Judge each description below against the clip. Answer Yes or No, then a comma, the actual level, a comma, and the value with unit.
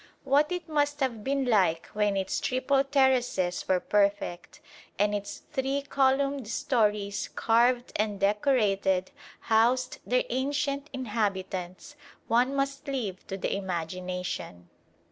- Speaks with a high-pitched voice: Yes, high, 230 Hz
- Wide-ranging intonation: Yes, wide, 5.7 semitones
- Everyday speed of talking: No, slow, 120 wpm